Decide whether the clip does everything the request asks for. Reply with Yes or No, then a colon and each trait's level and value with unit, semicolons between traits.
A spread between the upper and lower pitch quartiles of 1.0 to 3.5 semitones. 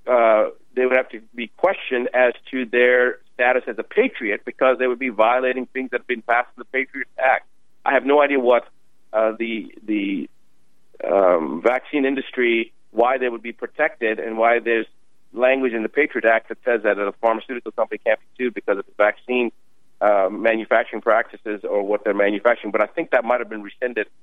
Yes: narrow, 2.5 semitones